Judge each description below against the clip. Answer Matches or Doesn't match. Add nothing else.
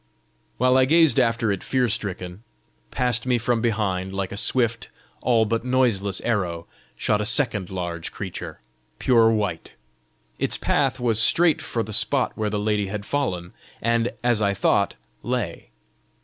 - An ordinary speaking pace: Matches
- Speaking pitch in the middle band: Doesn't match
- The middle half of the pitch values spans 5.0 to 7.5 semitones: Doesn't match